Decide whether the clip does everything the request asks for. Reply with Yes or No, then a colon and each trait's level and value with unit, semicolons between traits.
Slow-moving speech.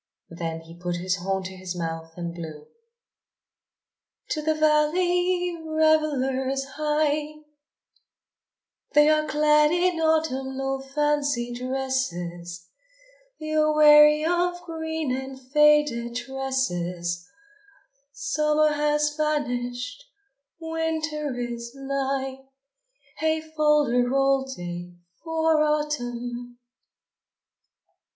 Yes: slow, 90 wpm